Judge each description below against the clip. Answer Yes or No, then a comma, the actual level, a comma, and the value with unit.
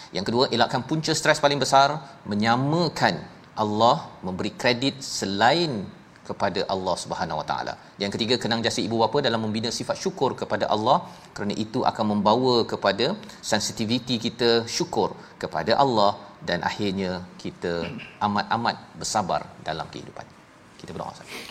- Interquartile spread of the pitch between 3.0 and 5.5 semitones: Yes, average, 3.4 semitones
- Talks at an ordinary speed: No, fast, 135 wpm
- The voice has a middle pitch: No, low, 115 Hz